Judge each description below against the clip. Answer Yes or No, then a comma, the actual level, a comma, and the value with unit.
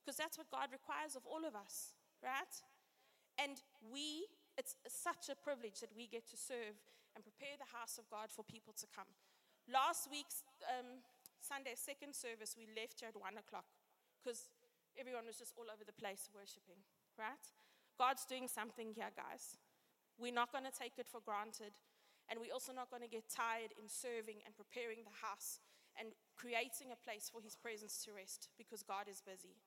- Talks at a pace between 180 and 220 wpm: Yes, average, 190 wpm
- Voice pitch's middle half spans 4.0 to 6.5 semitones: No, average, 3.5 semitones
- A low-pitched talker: No, high, 235 Hz